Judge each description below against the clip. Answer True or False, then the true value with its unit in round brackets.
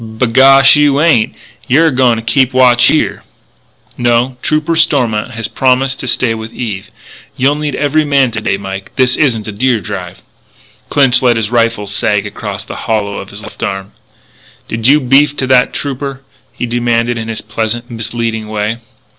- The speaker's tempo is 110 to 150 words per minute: False (175 wpm)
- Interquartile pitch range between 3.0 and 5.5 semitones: True (3.3 semitones)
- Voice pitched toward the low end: True (120 Hz)